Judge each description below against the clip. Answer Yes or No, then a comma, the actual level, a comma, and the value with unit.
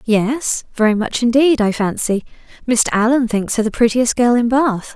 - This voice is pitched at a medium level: No, high, 235 Hz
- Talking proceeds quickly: No, average, 180 wpm